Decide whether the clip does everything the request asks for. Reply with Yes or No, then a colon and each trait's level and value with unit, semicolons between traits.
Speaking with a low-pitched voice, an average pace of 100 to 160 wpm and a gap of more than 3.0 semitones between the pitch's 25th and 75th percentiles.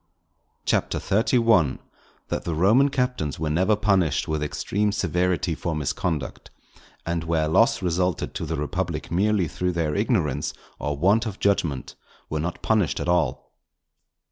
Yes: very low, 90 Hz; average, 140 wpm; average, 4.6 semitones